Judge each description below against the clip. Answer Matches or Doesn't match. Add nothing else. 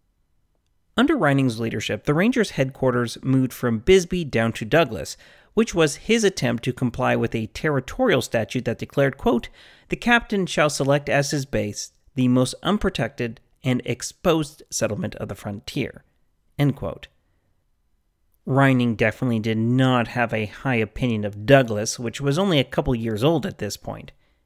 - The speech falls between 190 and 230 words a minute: Doesn't match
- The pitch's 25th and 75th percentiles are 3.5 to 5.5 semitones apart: Matches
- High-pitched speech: Doesn't match